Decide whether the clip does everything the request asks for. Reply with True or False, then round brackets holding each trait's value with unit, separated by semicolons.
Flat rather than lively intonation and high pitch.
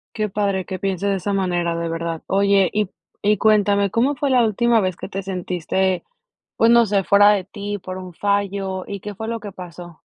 True (2.0 semitones; 200 Hz)